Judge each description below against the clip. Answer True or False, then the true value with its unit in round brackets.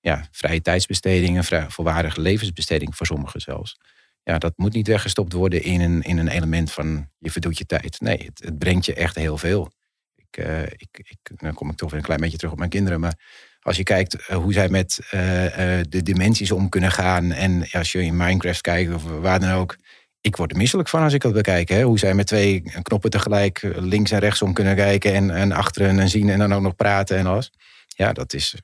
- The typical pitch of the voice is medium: False (90 Hz)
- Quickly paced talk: True (235 wpm)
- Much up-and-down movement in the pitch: False (3.0 semitones)